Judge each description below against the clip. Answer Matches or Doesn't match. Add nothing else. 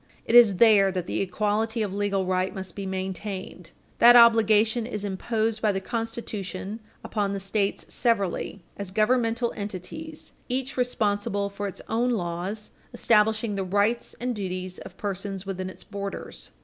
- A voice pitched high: Matches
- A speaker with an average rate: Matches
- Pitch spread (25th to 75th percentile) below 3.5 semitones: Matches